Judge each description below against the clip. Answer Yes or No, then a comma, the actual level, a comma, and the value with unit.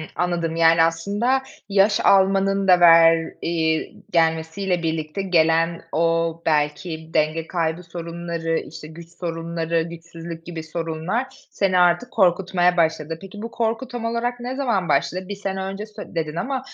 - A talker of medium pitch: Yes, medium, 170 Hz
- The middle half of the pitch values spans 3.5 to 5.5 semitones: No, average, 3.1 semitones